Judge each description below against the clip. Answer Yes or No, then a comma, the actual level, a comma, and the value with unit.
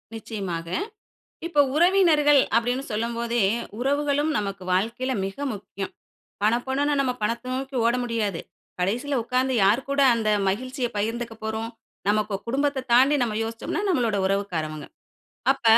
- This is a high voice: Yes, high, 235 Hz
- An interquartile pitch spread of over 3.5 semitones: Yes, average, 4.3 semitones